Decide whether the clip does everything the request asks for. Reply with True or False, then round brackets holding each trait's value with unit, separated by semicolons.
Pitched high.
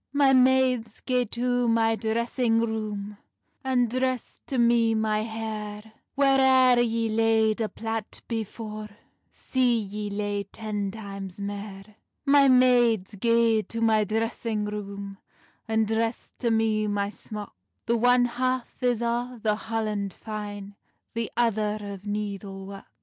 True (225 Hz)